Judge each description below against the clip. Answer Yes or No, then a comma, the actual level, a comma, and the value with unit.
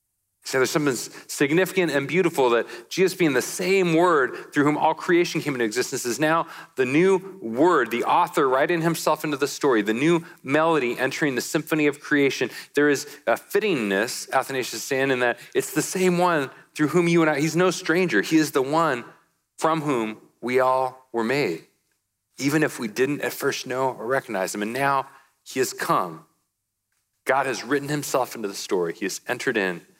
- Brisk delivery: No, average, 190 wpm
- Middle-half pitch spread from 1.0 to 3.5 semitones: No, average, 4.1 semitones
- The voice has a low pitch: No, medium, 150 Hz